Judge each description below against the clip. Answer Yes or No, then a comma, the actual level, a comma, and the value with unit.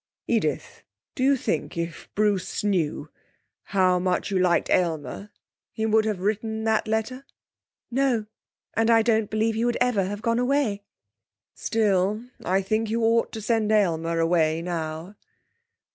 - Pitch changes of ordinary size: Yes, average, 3.7 semitones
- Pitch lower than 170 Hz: No, high, 210 Hz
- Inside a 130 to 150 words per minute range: Yes, average, 145 wpm